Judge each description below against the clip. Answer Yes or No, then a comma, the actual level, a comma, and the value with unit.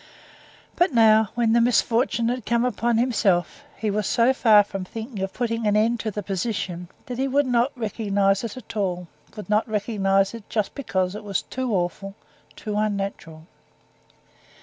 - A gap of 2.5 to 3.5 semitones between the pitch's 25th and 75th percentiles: Yes, average, 3.2 semitones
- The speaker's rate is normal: Yes, average, 170 wpm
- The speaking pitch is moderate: No, high, 215 Hz